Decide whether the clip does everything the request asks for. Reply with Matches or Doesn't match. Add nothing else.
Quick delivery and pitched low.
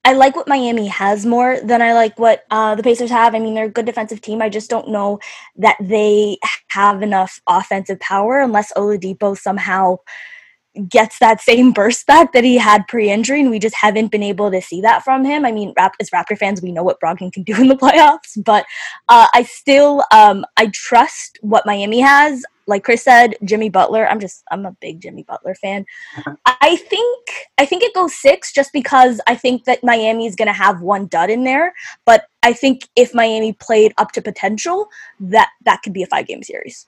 Doesn't match